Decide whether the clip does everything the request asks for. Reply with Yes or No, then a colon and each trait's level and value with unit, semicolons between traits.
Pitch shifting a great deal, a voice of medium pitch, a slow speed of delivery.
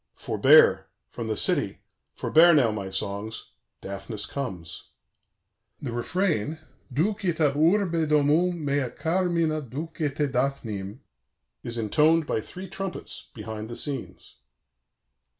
Yes: wide, 6.4 semitones; medium, 145 Hz; slow, 110 wpm